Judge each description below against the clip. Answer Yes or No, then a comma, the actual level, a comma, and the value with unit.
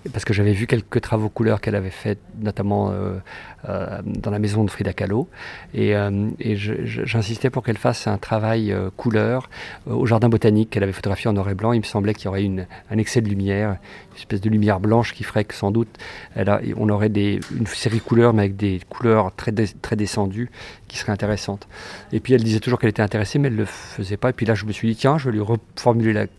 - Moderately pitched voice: No, low, 110 Hz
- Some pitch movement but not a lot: No, narrow, 2.0 semitones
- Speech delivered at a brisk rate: Yes, fast, 250 wpm